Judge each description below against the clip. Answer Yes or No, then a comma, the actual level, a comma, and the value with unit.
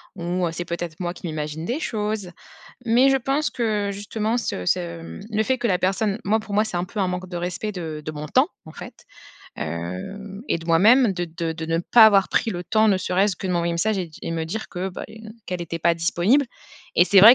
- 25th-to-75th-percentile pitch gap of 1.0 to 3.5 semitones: No, average, 4.2 semitones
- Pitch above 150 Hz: Yes, medium, 185 Hz